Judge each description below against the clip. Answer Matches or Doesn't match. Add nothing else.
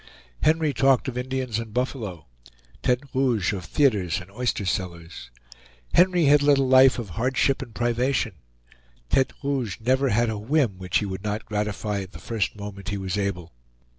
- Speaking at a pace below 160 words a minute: Doesn't match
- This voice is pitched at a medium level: Doesn't match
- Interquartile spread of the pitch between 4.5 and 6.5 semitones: Matches